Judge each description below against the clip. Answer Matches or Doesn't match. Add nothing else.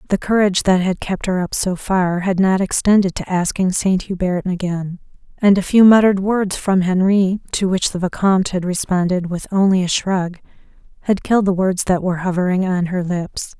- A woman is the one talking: Matches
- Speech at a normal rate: Matches